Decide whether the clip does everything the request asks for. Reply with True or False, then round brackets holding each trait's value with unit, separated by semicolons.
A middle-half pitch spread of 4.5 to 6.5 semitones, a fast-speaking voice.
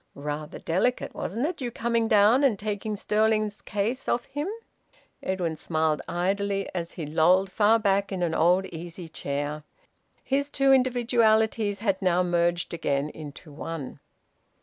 False (5.0 semitones; 145 wpm)